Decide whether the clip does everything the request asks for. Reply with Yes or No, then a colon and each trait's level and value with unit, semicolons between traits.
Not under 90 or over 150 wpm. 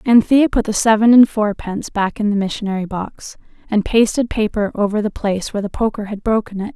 No: fast, 205 wpm